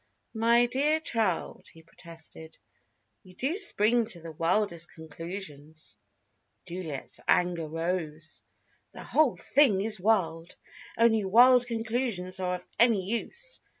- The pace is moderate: No, slow, 115 wpm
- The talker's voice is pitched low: No, high, 190 Hz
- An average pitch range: No, wide, 6.0 semitones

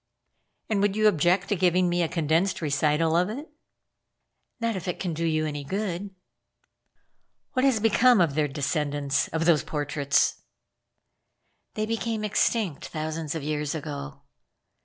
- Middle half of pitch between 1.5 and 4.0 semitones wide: No, average, 5.2 semitones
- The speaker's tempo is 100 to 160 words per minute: Yes, average, 145 wpm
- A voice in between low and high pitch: Yes, medium, 165 Hz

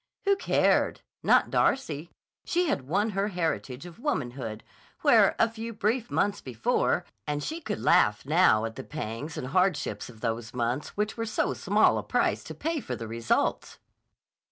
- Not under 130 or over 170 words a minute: Yes, average, 165 wpm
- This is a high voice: No, medium, 155 Hz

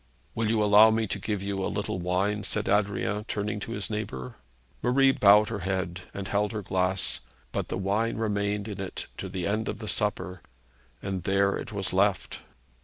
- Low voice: Yes, low, 100 Hz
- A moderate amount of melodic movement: No, narrow, 1.8 semitones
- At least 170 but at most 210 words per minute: Yes, average, 190 wpm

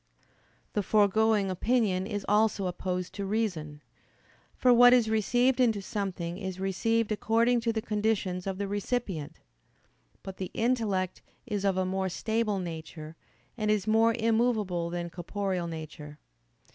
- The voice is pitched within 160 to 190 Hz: No, high, 200 Hz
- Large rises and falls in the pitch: No, average, 3.4 semitones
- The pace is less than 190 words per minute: Yes, average, 140 wpm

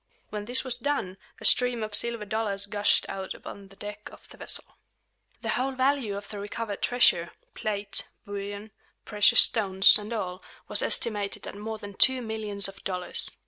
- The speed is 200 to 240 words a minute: No, average, 175 wpm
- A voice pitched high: Yes, high, 210 Hz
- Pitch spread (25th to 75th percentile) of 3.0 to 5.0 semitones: No, narrow, 2.4 semitones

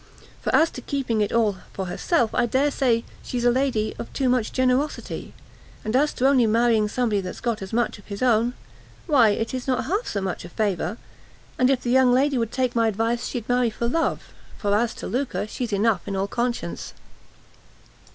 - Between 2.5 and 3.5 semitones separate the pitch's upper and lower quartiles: Yes, average, 3.0 semitones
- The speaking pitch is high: Yes, high, 235 Hz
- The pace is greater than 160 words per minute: Yes, fast, 205 wpm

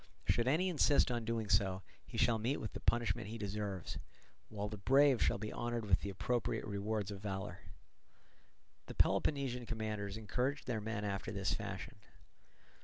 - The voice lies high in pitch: No, low, 110 Hz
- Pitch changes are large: No, average, 3.0 semitones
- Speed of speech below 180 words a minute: Yes, average, 165 wpm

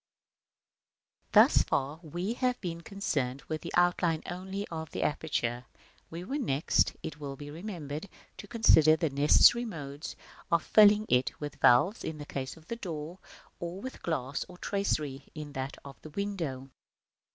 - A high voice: No, medium, 160 Hz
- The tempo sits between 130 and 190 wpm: Yes, average, 165 wpm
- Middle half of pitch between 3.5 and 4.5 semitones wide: No, average, 4.9 semitones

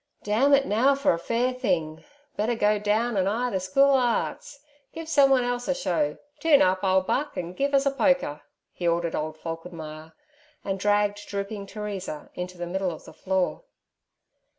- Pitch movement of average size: No, wide, 6.0 semitones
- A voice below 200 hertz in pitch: No, high, 205 Hz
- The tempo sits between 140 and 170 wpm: No, average, 180 wpm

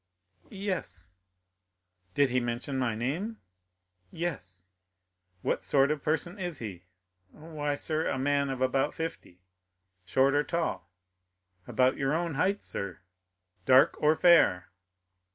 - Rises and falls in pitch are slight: No, average, 4.9 semitones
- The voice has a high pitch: No, medium, 140 Hz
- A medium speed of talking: No, slow, 120 wpm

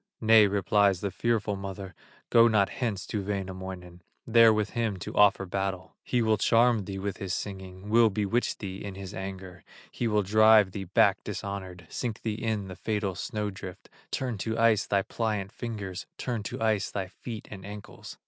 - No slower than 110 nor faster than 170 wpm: No, average, 180 wpm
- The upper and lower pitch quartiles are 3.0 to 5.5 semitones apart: No, narrow, 2.5 semitones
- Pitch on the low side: Yes, low, 100 Hz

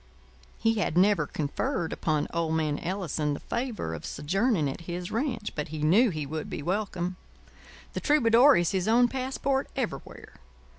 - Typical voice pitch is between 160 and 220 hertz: Yes, medium, 185 Hz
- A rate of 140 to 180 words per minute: Yes, average, 160 wpm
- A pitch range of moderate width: No, wide, 7.0 semitones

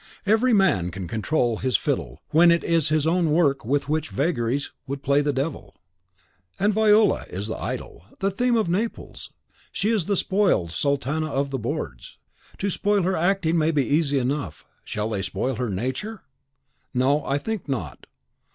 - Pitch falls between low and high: Yes, medium, 150 Hz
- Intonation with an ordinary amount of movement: No, wide, 6.7 semitones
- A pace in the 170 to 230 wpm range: Yes, average, 175 wpm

